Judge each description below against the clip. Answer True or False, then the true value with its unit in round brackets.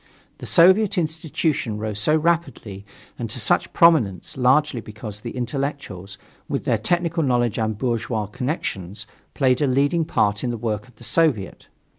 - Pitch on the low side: True (125 Hz)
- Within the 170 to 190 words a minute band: False (155 wpm)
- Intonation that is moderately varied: False (6.5 semitones)